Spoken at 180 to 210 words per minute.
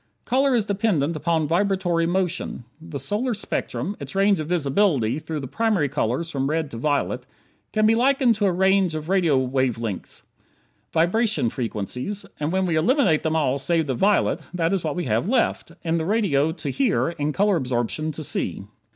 Yes: average, 185 wpm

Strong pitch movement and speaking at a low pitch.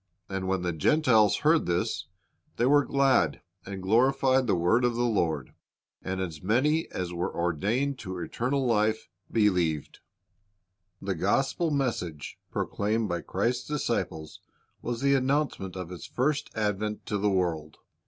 Yes: wide, 6.3 semitones; low, 105 Hz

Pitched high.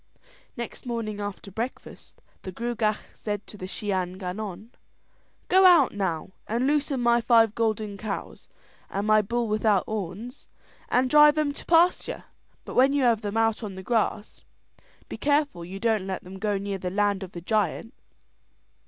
Yes: high, 215 Hz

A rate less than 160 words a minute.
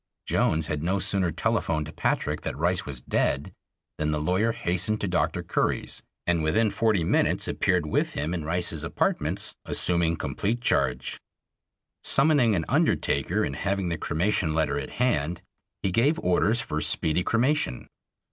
Yes: average, 150 wpm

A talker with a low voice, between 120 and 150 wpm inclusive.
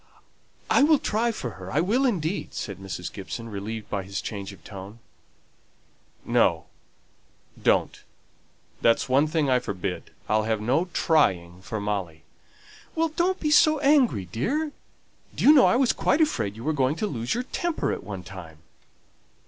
No: low, 115 Hz; average, 160 wpm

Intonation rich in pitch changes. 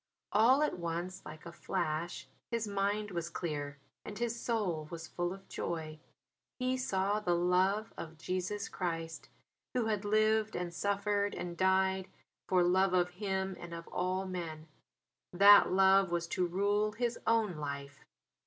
No: average, 3.2 semitones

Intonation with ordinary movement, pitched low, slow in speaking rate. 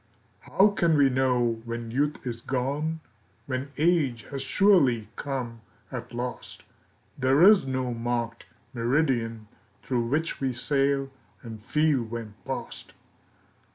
Yes: average, 3.5 semitones; low, 130 Hz; slow, 120 wpm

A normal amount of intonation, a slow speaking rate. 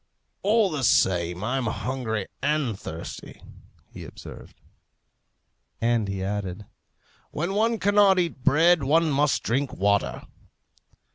No: wide, 8.5 semitones; slow, 115 wpm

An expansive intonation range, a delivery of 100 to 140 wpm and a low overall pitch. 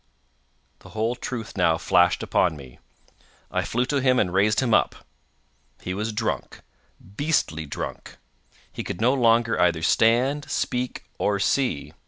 Yes: wide, 5.7 semitones; slow, 135 wpm; low, 110 Hz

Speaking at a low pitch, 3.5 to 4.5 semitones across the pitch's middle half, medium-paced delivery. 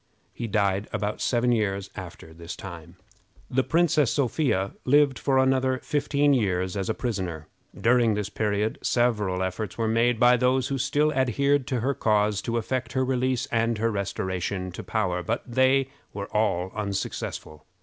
No: low, 115 Hz; average, 4.9 semitones; average, 155 wpm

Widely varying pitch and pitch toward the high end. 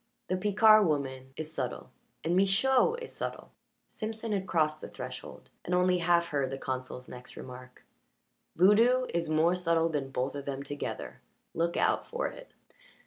No: wide, 6.3 semitones; medium, 170 Hz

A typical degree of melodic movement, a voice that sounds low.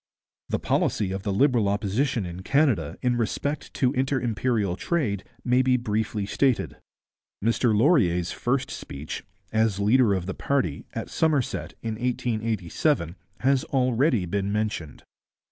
Yes: average, 4.6 semitones; low, 110 Hz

